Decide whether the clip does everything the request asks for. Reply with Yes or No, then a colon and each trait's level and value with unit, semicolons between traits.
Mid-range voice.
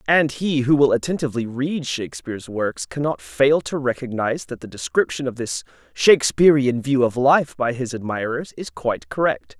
No: low, 130 Hz